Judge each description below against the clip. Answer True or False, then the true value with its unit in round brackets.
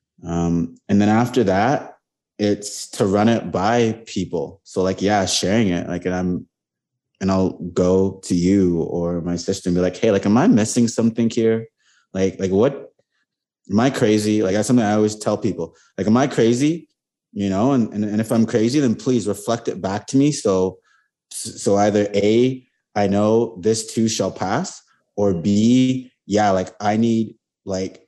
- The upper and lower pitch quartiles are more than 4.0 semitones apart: False (3.4 semitones)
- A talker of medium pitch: False (105 Hz)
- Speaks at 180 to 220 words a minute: True (185 wpm)